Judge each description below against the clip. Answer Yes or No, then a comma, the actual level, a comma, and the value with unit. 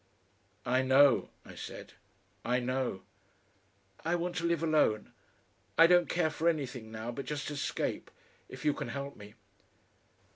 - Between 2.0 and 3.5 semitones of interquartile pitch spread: No, average, 4.9 semitones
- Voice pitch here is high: No, medium, 140 Hz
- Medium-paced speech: Yes, average, 145 wpm